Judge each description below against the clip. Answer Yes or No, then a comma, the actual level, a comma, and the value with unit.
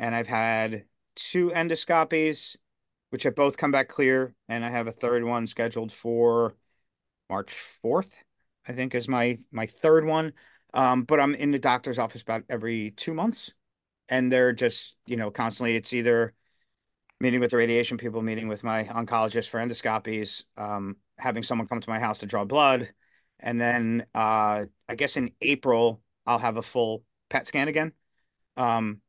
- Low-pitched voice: Yes, low, 115 Hz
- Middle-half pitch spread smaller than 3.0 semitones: Yes, narrow, 2.4 semitones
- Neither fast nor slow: Yes, average, 170 wpm